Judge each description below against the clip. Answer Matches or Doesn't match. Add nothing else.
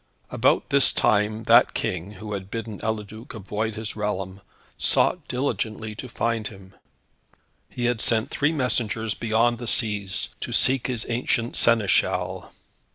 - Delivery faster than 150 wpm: Doesn't match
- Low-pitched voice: Matches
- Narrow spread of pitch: Matches